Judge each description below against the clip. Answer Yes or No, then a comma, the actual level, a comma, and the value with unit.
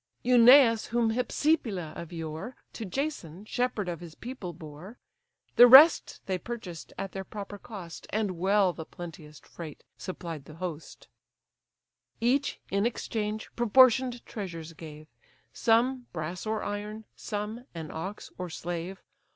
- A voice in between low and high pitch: No, high, 200 Hz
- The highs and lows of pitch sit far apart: Yes, wide, 5.9 semitones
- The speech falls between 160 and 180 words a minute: No, slow, 135 wpm